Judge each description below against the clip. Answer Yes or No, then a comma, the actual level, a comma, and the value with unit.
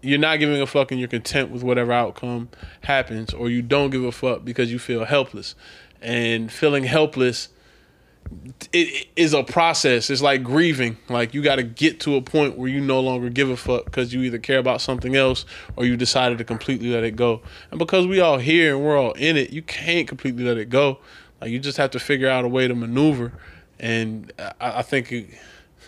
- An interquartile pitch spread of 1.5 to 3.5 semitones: Yes, average, 2.9 semitones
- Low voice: Yes, low, 130 Hz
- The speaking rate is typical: No, fast, 220 wpm